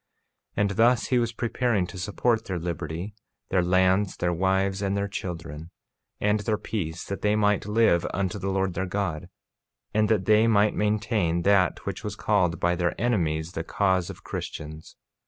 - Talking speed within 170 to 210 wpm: Yes, average, 180 wpm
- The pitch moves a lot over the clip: No, average, 3.1 semitones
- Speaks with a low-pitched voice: Yes, very low, 95 Hz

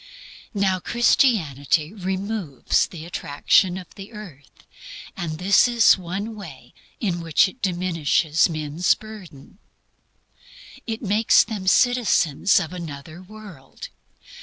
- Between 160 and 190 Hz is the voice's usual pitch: Yes, medium, 185 Hz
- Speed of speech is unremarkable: No, slow, 110 wpm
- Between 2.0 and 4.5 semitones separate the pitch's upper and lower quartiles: No, average, 5.0 semitones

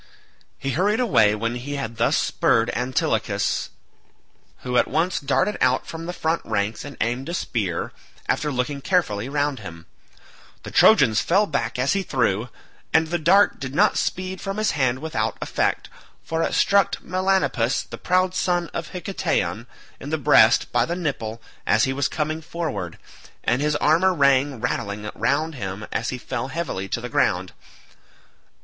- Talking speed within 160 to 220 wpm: Yes, average, 165 wpm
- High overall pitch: No, medium, 140 Hz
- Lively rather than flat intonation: Yes, wide, 6.5 semitones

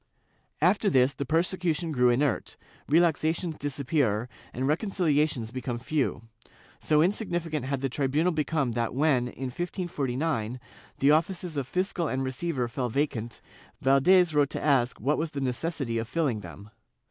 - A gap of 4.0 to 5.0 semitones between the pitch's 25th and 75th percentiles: Yes, average, 4.5 semitones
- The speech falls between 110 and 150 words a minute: Yes, average, 145 wpm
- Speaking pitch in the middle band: Yes, medium, 145 Hz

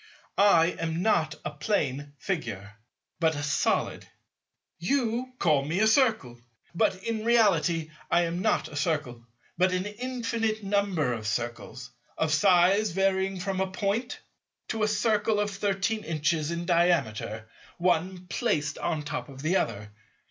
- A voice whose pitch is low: No, medium, 175 Hz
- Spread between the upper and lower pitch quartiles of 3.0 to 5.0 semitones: No, wide, 5.5 semitones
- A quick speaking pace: No, average, 150 wpm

